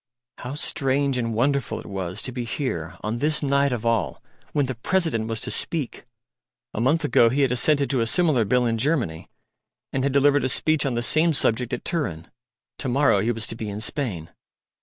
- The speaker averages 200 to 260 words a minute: Yes, fast, 205 wpm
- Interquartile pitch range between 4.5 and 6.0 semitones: No, average, 4.0 semitones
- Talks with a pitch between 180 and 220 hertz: No, low, 125 Hz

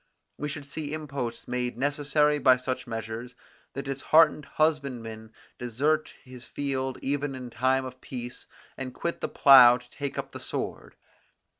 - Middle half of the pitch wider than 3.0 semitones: No, average, 2.7 semitones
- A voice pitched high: No, low, 130 Hz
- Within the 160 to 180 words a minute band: No, average, 150 wpm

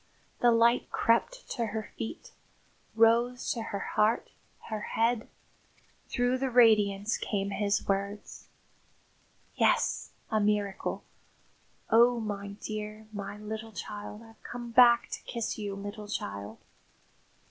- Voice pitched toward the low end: No, high, 220 Hz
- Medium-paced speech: No, slow, 120 wpm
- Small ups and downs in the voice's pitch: Yes, narrow, 2.3 semitones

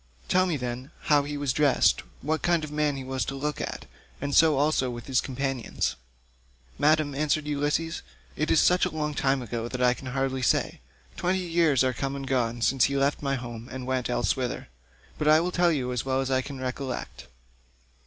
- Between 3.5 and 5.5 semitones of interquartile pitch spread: No, average, 2.8 semitones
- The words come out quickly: Yes, fast, 210 wpm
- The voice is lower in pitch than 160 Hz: Yes, low, 135 Hz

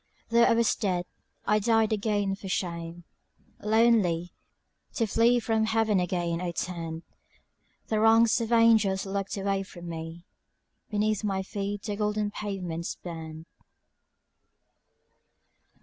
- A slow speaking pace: Yes, slow, 120 wpm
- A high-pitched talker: Yes, high, 200 Hz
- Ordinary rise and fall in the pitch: Yes, average, 3.9 semitones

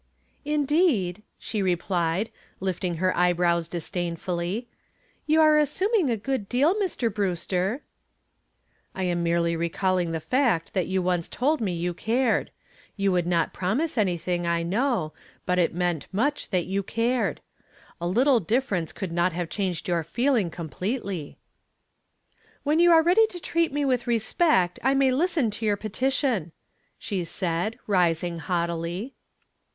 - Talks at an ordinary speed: Yes, average, 145 wpm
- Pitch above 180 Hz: Yes, high, 190 Hz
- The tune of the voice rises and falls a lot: Yes, wide, 7.0 semitones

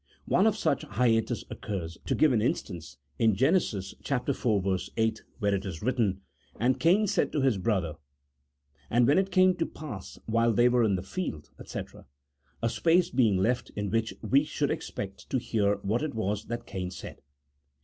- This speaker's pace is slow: No, average, 180 wpm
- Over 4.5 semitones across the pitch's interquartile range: Yes, average, 5.1 semitones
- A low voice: Yes, low, 115 Hz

